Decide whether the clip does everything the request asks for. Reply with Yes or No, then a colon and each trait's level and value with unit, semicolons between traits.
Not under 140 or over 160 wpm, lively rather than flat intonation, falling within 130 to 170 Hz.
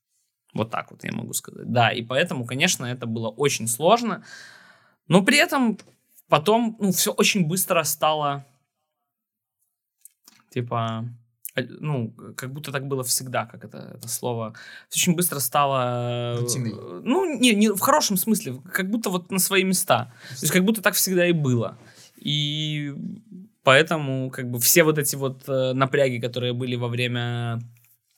Yes: average, 150 wpm; wide, 7.2 semitones; medium, 140 Hz